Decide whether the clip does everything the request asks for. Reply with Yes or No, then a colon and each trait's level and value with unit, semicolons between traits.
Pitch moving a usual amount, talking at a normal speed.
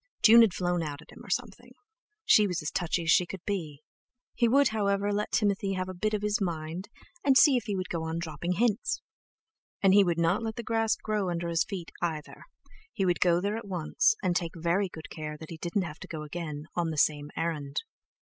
No: average, 3.9 semitones; fast, 230 wpm